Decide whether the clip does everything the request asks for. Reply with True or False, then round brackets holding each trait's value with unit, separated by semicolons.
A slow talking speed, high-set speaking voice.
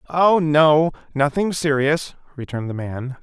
False (130 wpm; 145 Hz)